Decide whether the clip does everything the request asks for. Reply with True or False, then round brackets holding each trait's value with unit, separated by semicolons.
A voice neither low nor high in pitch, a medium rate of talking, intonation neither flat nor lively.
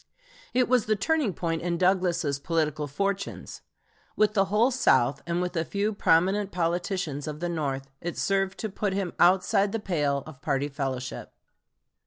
True (175 Hz; 165 wpm; 4.7 semitones)